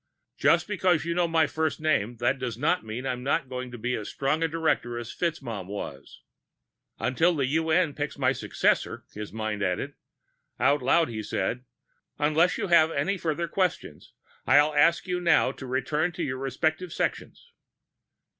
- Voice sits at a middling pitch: Yes, medium, 145 Hz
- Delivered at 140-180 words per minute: Yes, average, 165 wpm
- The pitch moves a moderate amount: Yes, average, 4.9 semitones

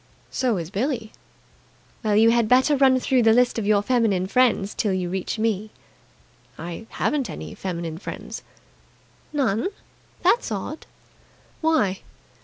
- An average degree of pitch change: Yes, average, 4.7 semitones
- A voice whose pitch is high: Yes, high, 220 Hz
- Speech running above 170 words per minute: No, slow, 135 wpm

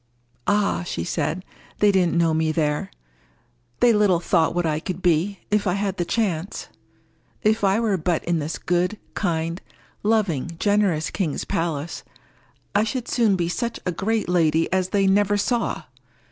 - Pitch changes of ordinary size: Yes, average, 3.7 semitones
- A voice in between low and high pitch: Yes, medium, 180 Hz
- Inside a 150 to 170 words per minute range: Yes, average, 160 wpm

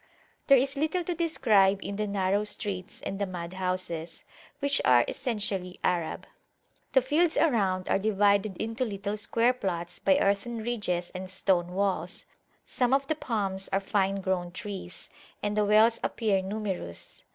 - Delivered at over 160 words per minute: No, average, 155 wpm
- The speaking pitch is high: Yes, high, 200 Hz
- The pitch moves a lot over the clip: No, average, 3.6 semitones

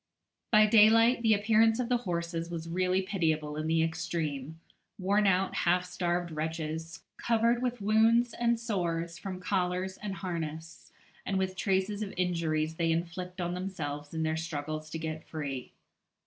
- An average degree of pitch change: Yes, average, 4.0 semitones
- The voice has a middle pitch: Yes, medium, 180 Hz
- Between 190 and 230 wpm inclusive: No, average, 155 wpm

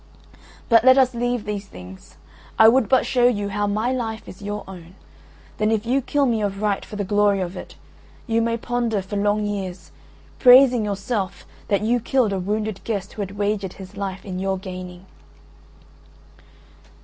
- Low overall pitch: No, high, 205 Hz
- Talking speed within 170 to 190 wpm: Yes, average, 180 wpm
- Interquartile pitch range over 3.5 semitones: No, average, 3.0 semitones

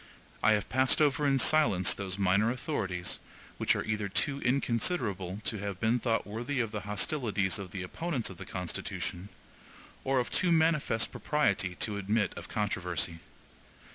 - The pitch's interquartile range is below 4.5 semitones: No, wide, 5.5 semitones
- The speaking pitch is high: No, low, 105 Hz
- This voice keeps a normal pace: Yes, average, 160 wpm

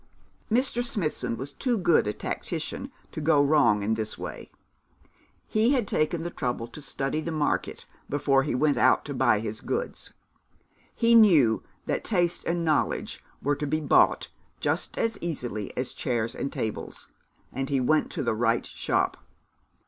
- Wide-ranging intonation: Yes, wide, 5.8 semitones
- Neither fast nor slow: Yes, average, 165 wpm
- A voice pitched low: No, medium, 145 Hz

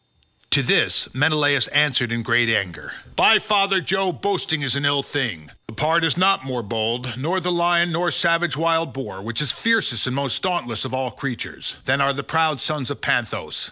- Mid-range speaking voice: Yes, medium, 145 Hz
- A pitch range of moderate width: No, wide, 5.7 semitones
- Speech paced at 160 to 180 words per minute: No, average, 190 wpm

